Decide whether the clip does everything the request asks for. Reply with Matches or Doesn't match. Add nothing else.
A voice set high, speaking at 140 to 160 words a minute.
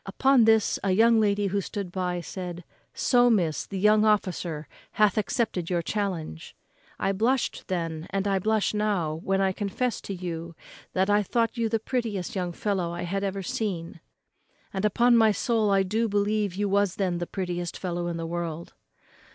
Doesn't match